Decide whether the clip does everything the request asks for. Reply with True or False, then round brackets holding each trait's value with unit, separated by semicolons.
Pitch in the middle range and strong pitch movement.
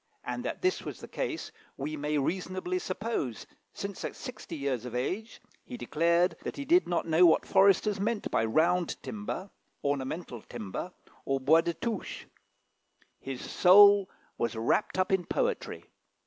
True (180 Hz; 6.1 semitones)